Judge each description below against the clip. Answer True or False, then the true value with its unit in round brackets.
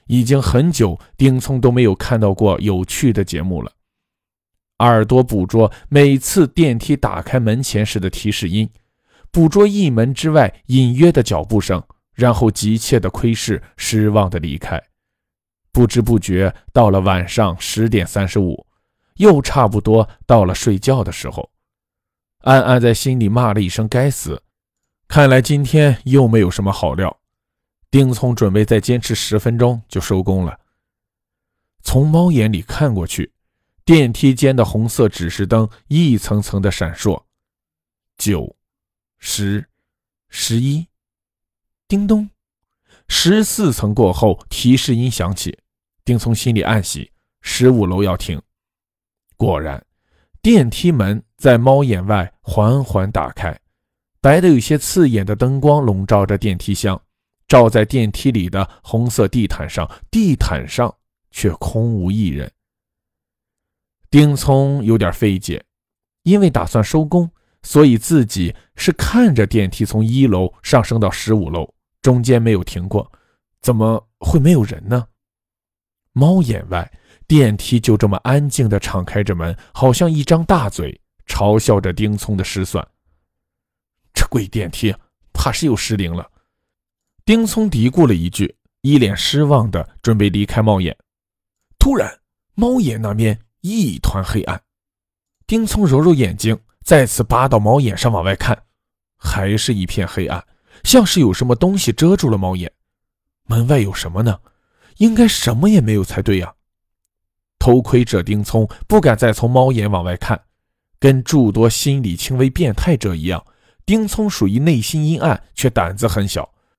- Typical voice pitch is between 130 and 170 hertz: False (110 Hz)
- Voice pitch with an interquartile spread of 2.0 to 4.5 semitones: False (5.3 semitones)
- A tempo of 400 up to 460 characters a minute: False (215 characters per minute)